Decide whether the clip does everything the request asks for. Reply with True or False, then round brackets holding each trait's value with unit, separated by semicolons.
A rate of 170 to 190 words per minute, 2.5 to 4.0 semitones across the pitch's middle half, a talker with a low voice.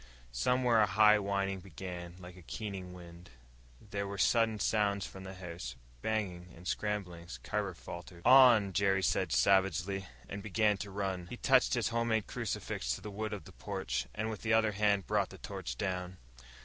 True (180 wpm; 2.8 semitones; 100 Hz)